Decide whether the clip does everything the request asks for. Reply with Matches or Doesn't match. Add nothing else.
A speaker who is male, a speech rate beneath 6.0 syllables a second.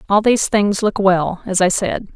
Doesn't match